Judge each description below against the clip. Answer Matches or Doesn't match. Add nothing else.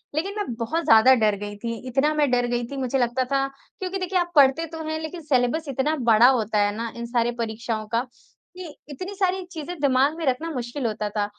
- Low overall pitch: Doesn't match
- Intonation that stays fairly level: Doesn't match